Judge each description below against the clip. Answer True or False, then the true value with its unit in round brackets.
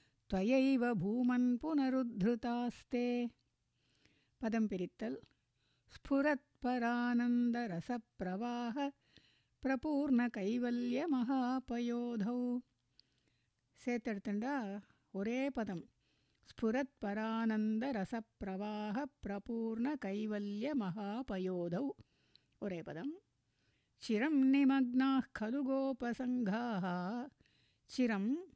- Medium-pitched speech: False (240 Hz)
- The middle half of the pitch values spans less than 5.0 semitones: True (3.9 semitones)